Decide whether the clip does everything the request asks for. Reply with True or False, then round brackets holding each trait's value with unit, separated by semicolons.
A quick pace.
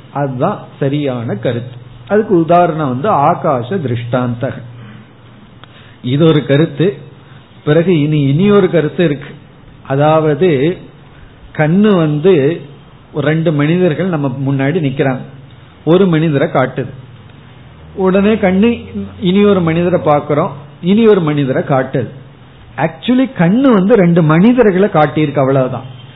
False (105 wpm)